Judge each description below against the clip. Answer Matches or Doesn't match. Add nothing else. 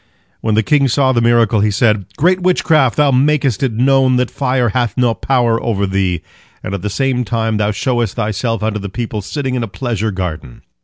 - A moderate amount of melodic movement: Matches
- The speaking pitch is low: Matches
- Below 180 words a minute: Doesn't match